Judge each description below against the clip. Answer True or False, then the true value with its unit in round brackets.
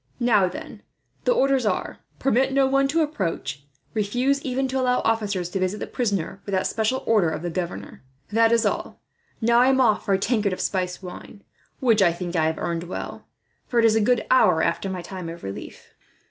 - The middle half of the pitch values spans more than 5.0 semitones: True (5.5 semitones)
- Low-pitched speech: False (210 Hz)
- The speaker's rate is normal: False (210 wpm)